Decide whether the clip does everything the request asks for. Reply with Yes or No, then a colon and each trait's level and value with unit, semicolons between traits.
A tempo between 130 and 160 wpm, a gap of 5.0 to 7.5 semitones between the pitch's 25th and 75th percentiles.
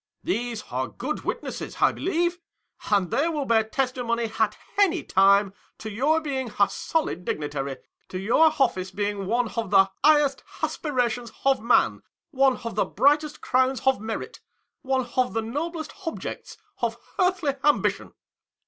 Yes: average, 150 wpm; wide, 5.6 semitones